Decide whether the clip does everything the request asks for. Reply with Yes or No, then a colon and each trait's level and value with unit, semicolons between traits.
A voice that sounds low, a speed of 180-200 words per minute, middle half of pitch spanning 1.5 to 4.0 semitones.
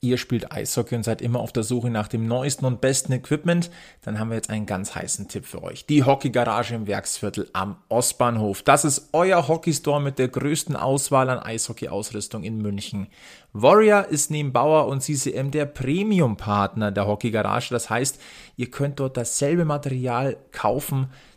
No: low, 130 Hz; average, 185 wpm; average, 4.4 semitones